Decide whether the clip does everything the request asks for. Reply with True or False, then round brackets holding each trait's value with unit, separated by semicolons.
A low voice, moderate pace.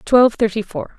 False (205 Hz; 185 wpm)